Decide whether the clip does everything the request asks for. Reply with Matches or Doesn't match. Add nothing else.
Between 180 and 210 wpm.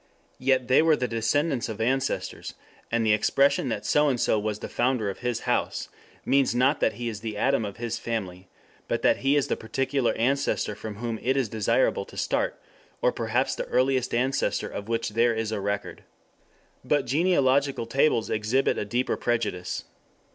Matches